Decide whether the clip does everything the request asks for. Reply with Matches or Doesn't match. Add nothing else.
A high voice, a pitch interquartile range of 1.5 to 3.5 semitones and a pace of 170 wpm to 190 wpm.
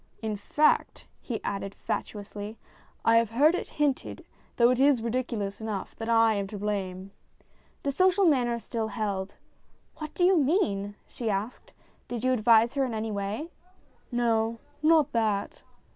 Doesn't match